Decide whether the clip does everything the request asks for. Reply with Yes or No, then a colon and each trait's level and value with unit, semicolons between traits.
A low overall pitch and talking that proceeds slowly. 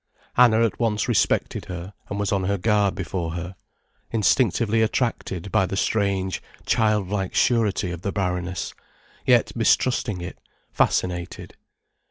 Yes: low, 100 Hz; slow, 130 wpm